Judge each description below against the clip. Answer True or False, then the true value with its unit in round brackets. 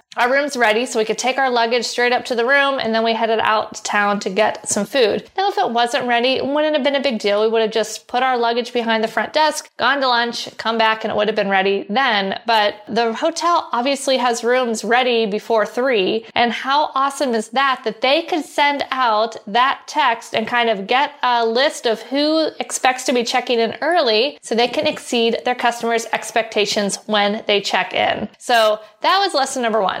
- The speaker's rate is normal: False (225 wpm)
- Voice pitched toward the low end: False (240 Hz)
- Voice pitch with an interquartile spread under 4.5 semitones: True (3.5 semitones)